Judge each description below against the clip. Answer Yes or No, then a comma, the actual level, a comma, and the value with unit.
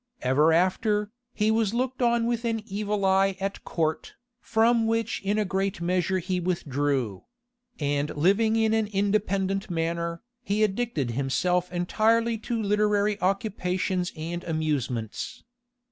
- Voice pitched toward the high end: Yes, high, 195 Hz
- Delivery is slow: Yes, slow, 130 wpm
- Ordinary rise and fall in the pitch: Yes, average, 4.4 semitones